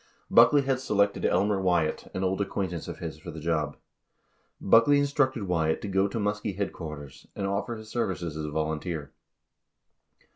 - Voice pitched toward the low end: Yes, very low, 95 Hz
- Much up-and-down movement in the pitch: No, average, 4.8 semitones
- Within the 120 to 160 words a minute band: No, average, 170 wpm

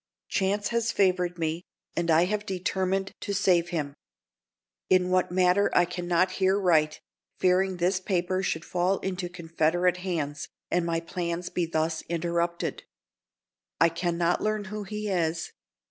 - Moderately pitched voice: Yes, medium, 180 Hz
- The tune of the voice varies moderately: No, narrow, 2.0 semitones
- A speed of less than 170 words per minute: Yes, average, 150 wpm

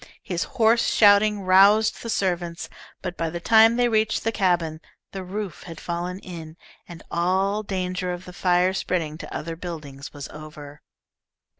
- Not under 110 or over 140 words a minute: No, average, 160 wpm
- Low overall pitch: No, medium, 180 Hz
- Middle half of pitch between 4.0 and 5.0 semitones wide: No, average, 3.3 semitones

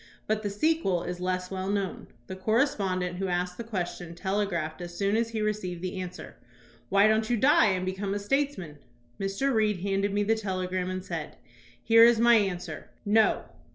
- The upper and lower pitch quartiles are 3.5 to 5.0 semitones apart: No, average, 3.1 semitones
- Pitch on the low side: No, high, 195 Hz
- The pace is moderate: Yes, average, 185 wpm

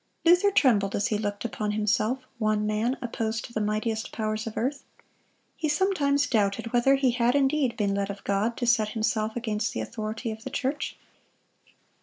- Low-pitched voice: No, high, 225 Hz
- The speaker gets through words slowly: No, average, 175 wpm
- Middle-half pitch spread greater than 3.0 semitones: Yes, average, 3.4 semitones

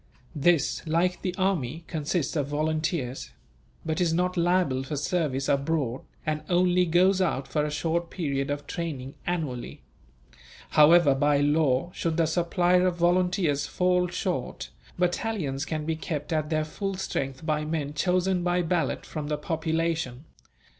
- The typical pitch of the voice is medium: Yes, medium, 160 Hz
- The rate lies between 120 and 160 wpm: Yes, average, 145 wpm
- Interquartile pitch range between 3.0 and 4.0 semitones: Yes, average, 3.4 semitones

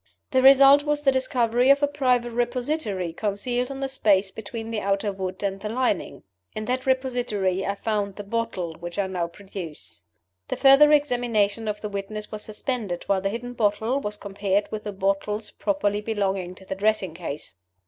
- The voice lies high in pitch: Yes, high, 210 Hz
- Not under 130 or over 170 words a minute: No, average, 180 wpm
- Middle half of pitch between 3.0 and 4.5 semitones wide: Yes, average, 4.1 semitones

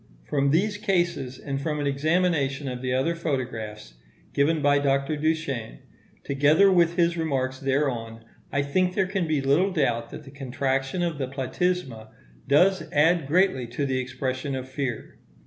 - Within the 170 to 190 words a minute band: No, average, 160 wpm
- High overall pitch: No, medium, 140 Hz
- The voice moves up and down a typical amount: Yes, average, 4.2 semitones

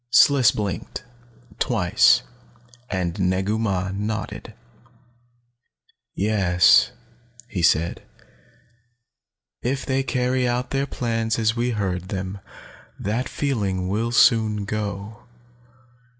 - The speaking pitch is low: Yes, low, 105 Hz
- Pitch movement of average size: Yes, average, 4.0 semitones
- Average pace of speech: No, slow, 95 wpm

